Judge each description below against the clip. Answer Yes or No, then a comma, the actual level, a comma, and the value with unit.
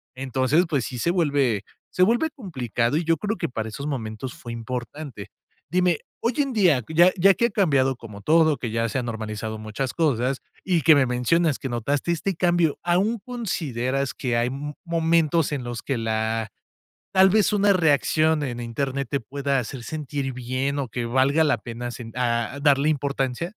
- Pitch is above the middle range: No, medium, 140 Hz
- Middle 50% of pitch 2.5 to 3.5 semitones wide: No, wide, 5.5 semitones